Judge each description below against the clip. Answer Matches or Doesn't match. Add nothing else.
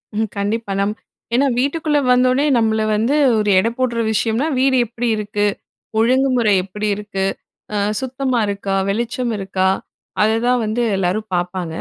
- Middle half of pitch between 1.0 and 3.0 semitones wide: Doesn't match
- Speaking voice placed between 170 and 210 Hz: Doesn't match